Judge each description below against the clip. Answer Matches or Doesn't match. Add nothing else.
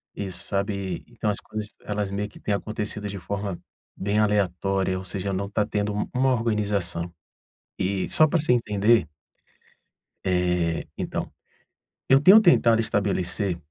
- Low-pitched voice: Matches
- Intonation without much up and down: Matches